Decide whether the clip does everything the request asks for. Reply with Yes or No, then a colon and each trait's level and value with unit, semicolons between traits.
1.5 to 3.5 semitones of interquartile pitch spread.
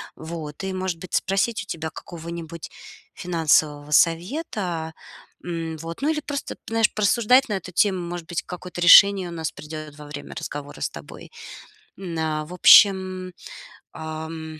Yes: average, 3.0 semitones